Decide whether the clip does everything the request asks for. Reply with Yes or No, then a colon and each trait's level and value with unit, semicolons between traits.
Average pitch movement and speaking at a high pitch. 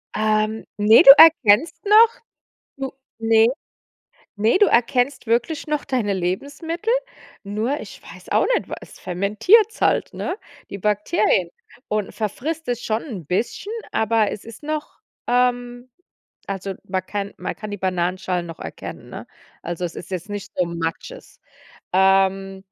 No: wide, 5.8 semitones; high, 215 Hz